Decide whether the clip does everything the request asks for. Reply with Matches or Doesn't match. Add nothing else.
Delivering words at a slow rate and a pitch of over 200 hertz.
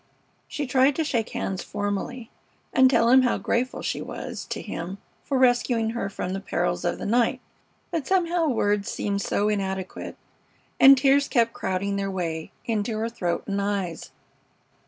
Doesn't match